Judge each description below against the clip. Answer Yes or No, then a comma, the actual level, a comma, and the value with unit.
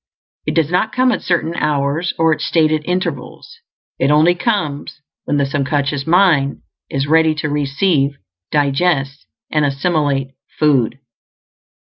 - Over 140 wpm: No, slow, 135 wpm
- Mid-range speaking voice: Yes, medium, 150 Hz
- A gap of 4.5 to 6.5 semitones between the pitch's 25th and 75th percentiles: No, average, 3.3 semitones